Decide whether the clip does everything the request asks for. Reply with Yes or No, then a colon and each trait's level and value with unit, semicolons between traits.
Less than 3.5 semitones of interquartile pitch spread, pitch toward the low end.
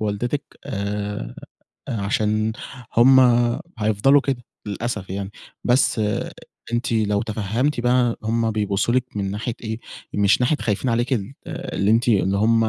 Yes: average, 2.9 semitones; low, 110 Hz